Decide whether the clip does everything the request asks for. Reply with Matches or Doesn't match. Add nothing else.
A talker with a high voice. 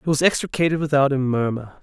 Doesn't match